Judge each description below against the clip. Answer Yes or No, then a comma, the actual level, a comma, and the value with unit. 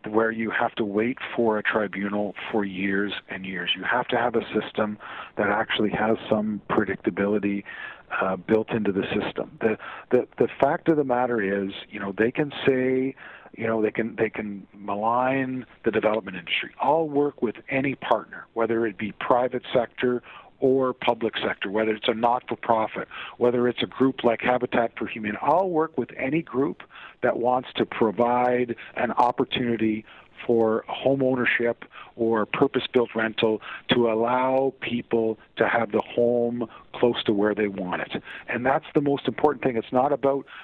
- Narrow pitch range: No, average, 3.0 semitones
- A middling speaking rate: Yes, average, 175 wpm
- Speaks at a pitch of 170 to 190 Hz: No, low, 115 Hz